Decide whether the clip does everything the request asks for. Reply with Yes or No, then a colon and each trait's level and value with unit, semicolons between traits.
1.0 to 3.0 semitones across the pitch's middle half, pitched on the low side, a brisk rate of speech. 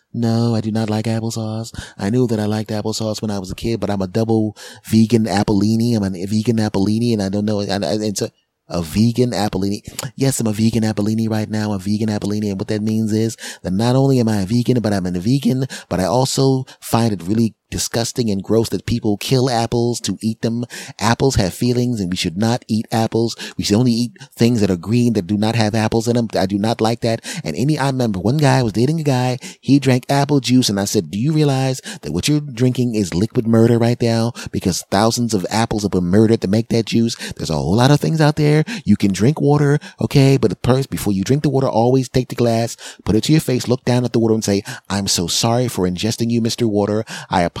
Yes: average, 2.7 semitones; low, 115 Hz; fast, 245 wpm